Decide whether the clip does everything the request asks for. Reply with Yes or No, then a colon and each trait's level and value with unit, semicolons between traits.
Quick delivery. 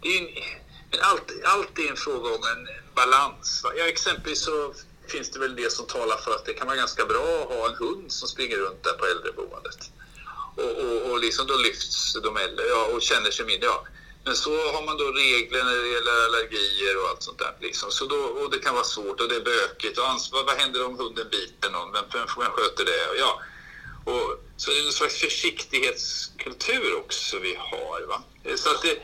Yes: fast, 215 wpm